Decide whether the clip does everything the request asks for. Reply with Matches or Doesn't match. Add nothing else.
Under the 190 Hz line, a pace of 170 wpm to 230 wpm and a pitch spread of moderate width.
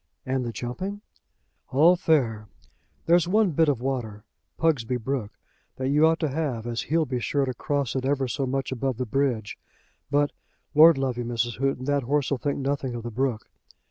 Matches